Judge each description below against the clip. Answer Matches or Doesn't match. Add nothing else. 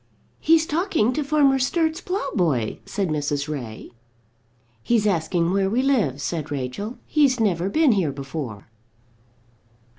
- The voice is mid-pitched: Doesn't match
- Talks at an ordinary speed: Doesn't match